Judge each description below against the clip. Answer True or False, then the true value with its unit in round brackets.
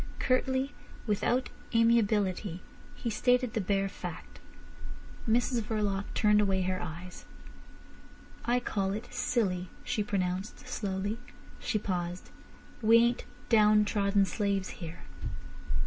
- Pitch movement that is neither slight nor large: True (3.3 semitones)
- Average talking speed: False (105 wpm)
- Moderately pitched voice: False (205 Hz)